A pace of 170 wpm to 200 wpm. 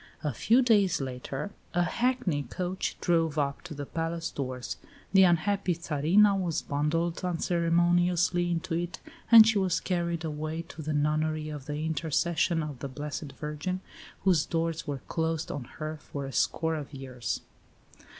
No: average, 155 wpm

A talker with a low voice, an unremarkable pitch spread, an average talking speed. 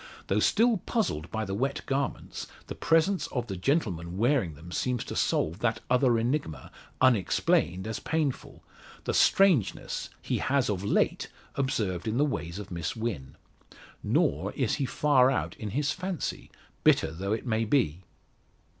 No: low, 120 Hz; wide, 7.0 semitones; average, 155 wpm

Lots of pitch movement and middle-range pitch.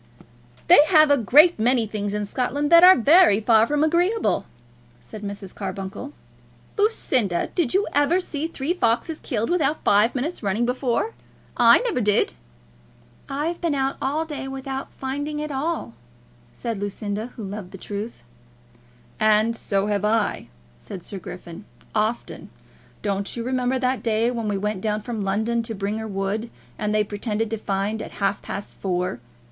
No: wide, 5.7 semitones; high, 230 Hz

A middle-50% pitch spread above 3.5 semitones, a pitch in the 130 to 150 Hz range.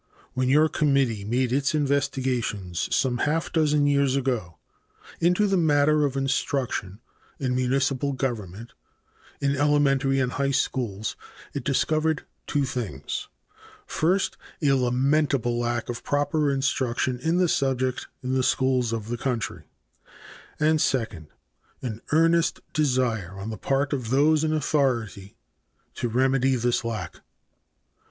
No: average, 3.2 semitones; low, 135 Hz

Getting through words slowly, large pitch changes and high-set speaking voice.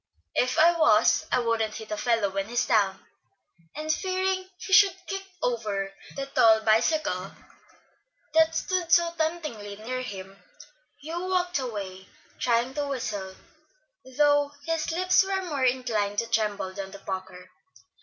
No: average, 145 wpm; wide, 7.9 semitones; high, 245 Hz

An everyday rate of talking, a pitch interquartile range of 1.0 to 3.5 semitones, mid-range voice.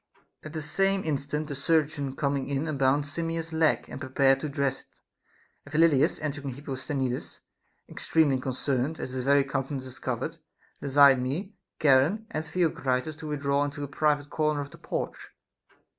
Yes: average, 170 wpm; narrow, 2.4 semitones; medium, 145 Hz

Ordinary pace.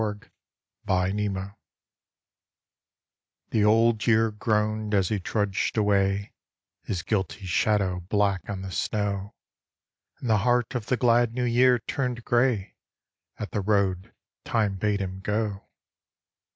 No: slow, 125 wpm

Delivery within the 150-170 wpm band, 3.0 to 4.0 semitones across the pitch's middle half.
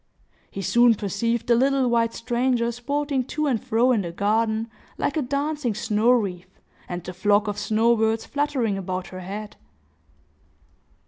Yes: average, 155 wpm; average, 3.5 semitones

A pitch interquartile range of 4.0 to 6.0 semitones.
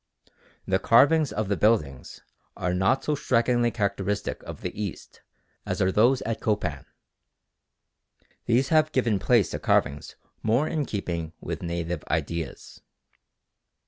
Yes: wide, 5.4 semitones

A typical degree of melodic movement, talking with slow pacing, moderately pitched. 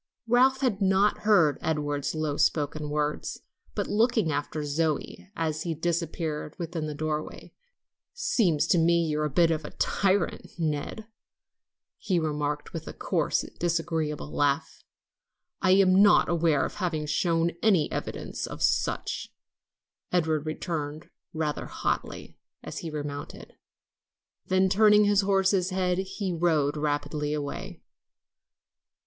Yes: average, 3.8 semitones; slow, 130 wpm; medium, 165 Hz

